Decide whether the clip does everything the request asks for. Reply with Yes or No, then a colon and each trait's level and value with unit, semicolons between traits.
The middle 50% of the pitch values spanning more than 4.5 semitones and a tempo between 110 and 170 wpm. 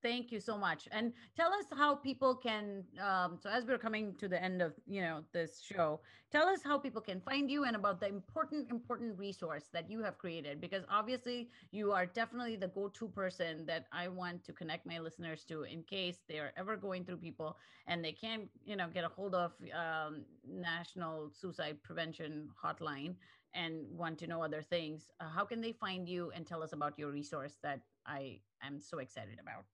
No: average, 5.1 semitones; fast, 205 wpm